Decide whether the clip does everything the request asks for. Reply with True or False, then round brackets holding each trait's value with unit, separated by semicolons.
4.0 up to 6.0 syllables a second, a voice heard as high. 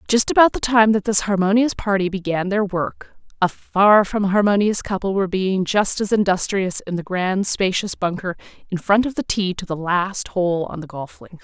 True (4.9 syllables/s; 195 Hz)